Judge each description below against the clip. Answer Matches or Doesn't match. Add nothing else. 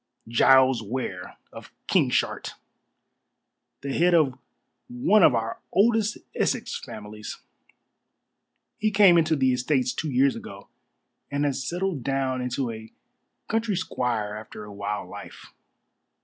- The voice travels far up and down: Matches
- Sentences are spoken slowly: Matches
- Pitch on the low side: Matches